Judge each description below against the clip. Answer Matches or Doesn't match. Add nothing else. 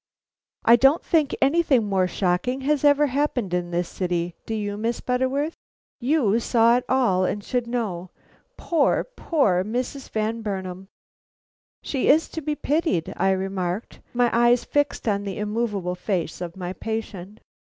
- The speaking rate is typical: Matches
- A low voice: Doesn't match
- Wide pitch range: Matches